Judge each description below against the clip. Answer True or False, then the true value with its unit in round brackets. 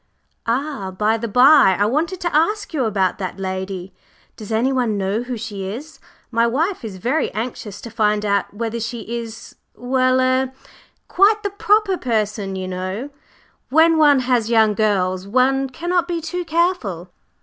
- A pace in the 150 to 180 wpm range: True (160 wpm)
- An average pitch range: False (6.4 semitones)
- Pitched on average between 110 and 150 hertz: False (235 Hz)